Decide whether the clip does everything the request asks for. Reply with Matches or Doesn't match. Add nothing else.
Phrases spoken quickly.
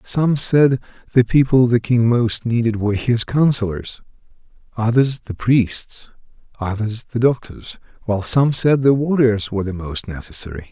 Doesn't match